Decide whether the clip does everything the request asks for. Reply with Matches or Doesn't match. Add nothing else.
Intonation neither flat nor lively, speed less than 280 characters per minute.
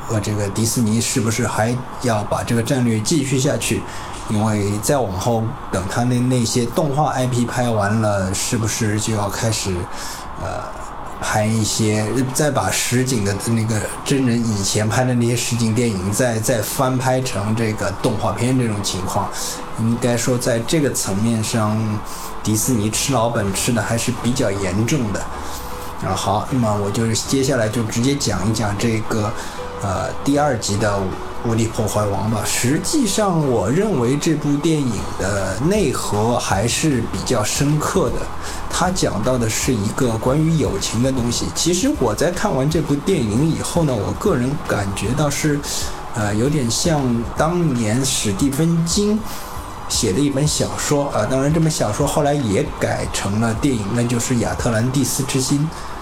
Matches